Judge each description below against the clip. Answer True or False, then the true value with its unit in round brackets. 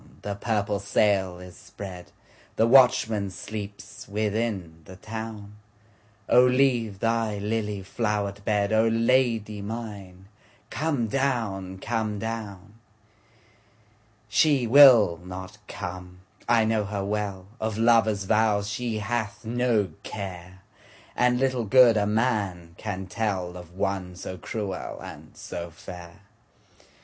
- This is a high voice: False (105 Hz)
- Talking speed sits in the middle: False (100 wpm)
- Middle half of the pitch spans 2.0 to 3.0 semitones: True (2.6 semitones)